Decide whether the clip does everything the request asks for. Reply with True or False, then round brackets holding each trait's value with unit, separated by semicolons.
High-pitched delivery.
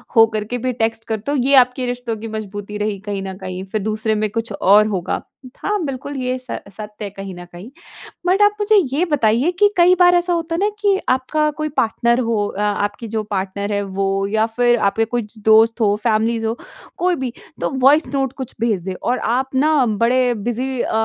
True (230 Hz)